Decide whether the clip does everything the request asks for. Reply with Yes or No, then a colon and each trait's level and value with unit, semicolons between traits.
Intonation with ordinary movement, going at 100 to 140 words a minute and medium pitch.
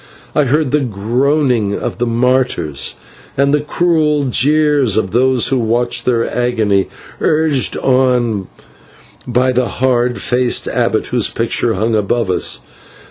No: average, 3.1 semitones; slow, 135 wpm; low, 125 Hz